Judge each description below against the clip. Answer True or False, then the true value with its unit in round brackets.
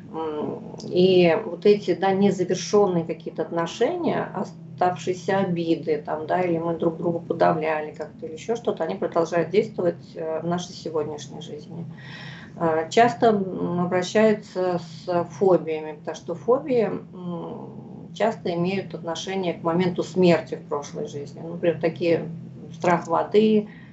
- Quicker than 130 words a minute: False (120 wpm)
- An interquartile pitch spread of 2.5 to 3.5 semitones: True (2.8 semitones)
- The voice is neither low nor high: True (170 Hz)